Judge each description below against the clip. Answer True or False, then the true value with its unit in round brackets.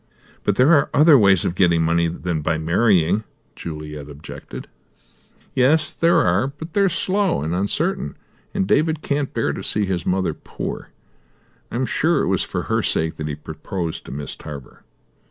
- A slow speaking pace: False (175 wpm)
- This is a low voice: True (95 Hz)